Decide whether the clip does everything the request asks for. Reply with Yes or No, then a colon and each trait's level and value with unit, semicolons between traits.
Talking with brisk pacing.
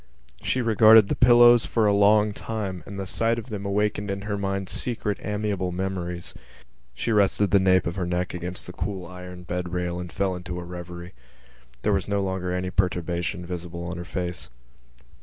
No: average, 190 wpm